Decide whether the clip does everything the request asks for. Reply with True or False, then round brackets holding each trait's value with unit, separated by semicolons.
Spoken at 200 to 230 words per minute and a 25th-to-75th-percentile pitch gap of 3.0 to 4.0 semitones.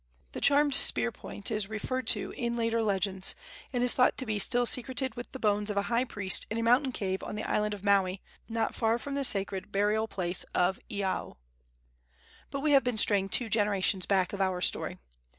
True (205 wpm; 3.7 semitones)